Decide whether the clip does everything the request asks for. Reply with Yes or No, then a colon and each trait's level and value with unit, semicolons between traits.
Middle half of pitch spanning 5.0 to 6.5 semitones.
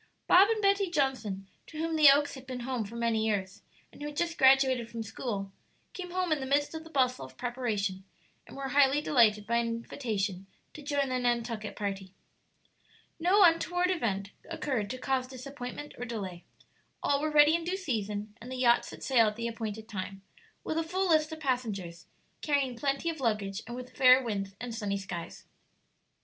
Yes: wide, 5.4 semitones